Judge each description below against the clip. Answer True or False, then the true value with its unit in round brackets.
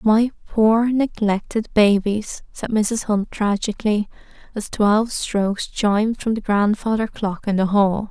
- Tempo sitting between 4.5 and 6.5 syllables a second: False (4.1 syllables/s)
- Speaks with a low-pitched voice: False (210 Hz)